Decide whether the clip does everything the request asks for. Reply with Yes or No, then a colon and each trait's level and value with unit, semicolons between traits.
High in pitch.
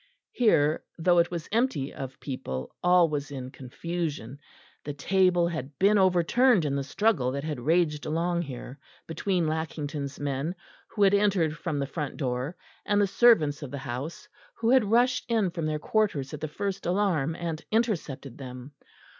No: medium, 160 Hz